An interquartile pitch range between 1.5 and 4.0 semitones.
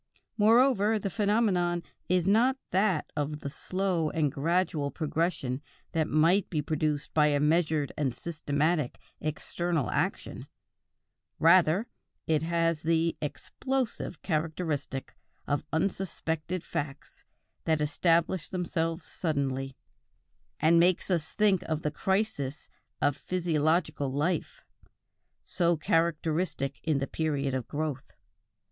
Yes: average, 3.3 semitones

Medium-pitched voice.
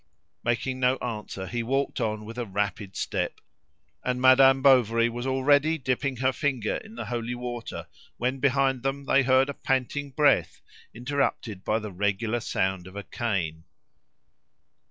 No: low, 125 Hz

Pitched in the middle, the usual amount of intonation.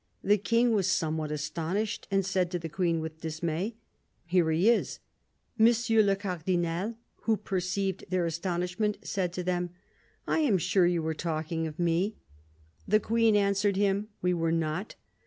Yes: medium, 180 Hz; average, 3.4 semitones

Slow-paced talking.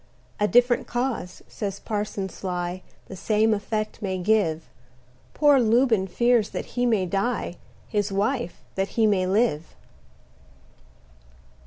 Yes: slow, 125 wpm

